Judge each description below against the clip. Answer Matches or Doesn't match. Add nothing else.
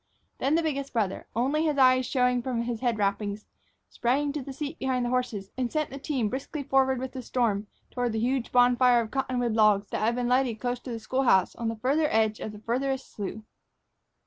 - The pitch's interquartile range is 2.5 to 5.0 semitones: Matches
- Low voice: Doesn't match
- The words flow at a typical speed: Doesn't match